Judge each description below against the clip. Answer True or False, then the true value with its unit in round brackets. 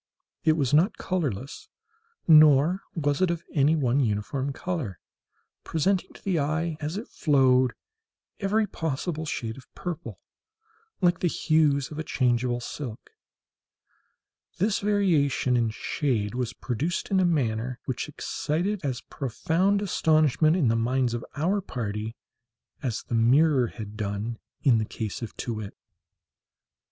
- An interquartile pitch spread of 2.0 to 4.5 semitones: False (5.4 semitones)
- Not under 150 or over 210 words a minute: False (135 wpm)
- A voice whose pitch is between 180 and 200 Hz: False (140 Hz)